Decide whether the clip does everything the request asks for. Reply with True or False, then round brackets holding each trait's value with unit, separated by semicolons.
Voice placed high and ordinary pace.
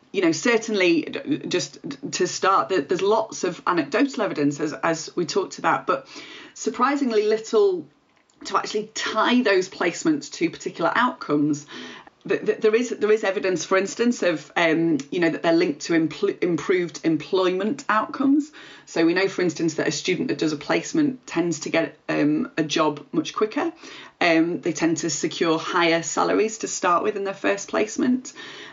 True (220 Hz; 165 wpm)